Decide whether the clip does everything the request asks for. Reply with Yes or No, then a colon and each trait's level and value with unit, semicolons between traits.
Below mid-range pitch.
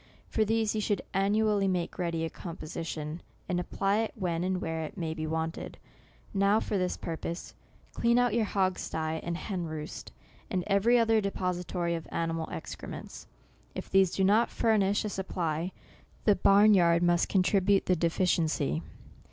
No: medium, 185 Hz